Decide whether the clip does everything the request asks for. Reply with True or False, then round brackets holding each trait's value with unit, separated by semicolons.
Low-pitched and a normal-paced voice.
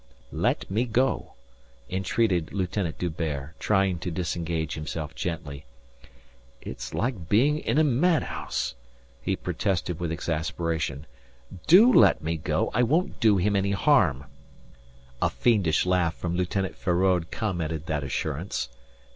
False (90 Hz; 125 wpm)